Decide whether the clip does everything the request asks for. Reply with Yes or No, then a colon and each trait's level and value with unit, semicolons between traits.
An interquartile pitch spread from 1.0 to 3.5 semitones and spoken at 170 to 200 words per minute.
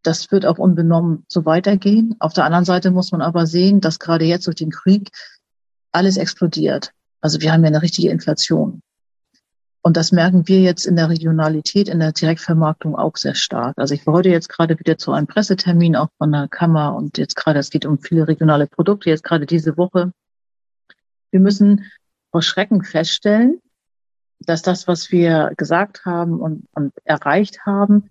Yes: average, 2.9 semitones; average, 180 wpm